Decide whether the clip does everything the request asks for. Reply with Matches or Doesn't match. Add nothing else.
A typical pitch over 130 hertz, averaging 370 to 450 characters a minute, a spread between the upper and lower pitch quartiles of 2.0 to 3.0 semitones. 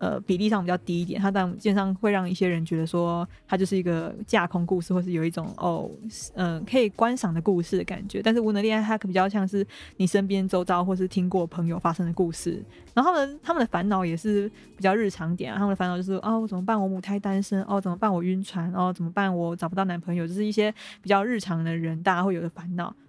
Matches